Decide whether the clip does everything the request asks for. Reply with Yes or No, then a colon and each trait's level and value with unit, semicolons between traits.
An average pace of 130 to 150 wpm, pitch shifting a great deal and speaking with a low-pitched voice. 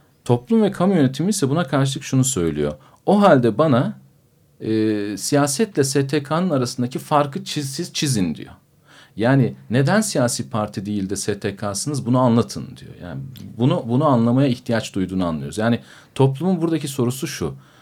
Yes: fast, 140 wpm; wide, 5.7 semitones; low, 130 Hz